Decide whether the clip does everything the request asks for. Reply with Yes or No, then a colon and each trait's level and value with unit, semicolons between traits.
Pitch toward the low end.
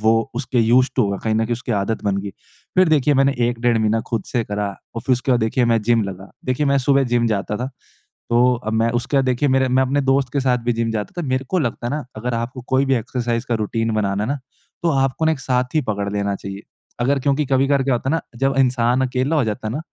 Yes: low, 125 Hz